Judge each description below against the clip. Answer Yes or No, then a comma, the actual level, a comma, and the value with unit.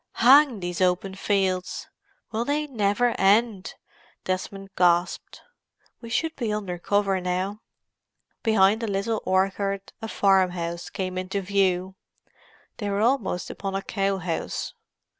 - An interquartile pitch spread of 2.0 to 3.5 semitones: Yes, average, 2.7 semitones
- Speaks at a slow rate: Yes, slow, 125 wpm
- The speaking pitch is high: Yes, high, 195 Hz